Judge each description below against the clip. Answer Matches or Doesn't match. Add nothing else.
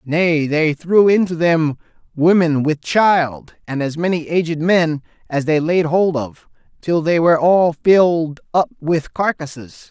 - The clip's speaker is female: Doesn't match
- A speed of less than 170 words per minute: Matches